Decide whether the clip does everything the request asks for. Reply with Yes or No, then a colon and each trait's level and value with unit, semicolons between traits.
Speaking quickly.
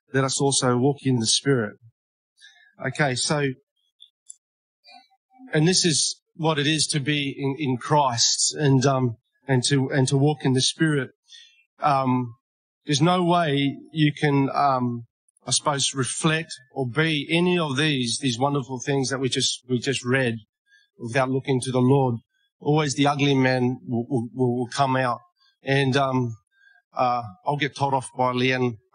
No: average, 160 wpm